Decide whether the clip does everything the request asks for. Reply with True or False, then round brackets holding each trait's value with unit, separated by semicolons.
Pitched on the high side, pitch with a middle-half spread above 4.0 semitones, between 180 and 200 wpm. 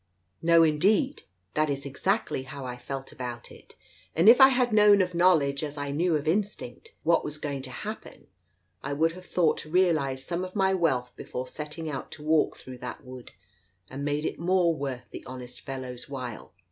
False (150 Hz; 5.1 semitones; 195 wpm)